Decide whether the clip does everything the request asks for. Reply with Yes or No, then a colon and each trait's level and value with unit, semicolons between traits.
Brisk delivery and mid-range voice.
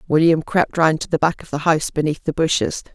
Yes: fast, 245 wpm; medium, 160 Hz